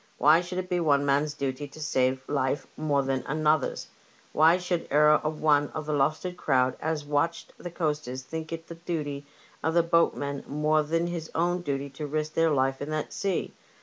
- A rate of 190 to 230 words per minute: Yes, average, 195 wpm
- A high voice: No, medium, 150 Hz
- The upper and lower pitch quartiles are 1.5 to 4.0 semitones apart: Yes, narrow, 2.6 semitones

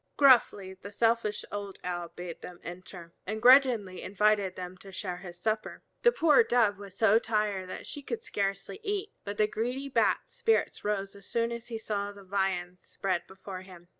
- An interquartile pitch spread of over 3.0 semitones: Yes, average, 3.7 semitones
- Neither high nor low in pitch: No, high, 200 Hz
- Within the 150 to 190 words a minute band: Yes, average, 185 wpm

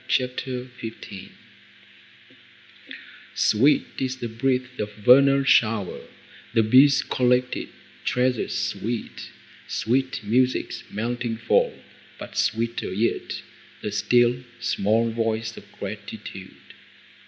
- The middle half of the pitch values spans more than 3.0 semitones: No, narrow, 2.5 semitones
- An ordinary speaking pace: No, slow, 95 wpm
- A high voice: No, low, 120 Hz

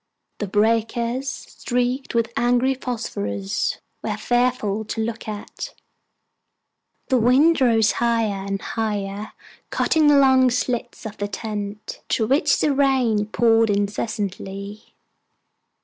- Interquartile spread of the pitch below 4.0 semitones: Yes, average, 3.4 semitones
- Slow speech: Yes, slow, 110 wpm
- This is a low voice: No, high, 230 Hz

